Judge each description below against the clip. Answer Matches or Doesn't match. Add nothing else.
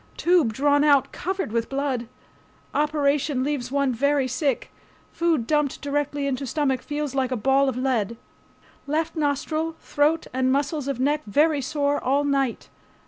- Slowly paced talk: Doesn't match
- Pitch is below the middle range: Doesn't match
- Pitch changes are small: Matches